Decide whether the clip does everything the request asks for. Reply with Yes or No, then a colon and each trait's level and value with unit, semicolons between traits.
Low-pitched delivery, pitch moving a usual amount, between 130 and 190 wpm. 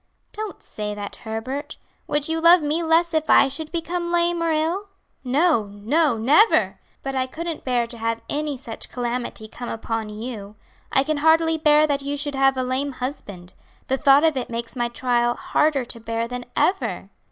No: very high, 275 Hz; average, 5.0 semitones; average, 185 wpm